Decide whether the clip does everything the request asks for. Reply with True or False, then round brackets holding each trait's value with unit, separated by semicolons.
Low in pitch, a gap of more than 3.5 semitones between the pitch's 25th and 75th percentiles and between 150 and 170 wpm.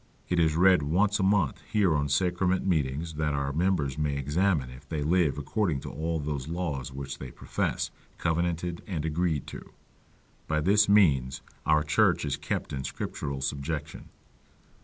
True (75 Hz; 4.0 semitones; 160 wpm)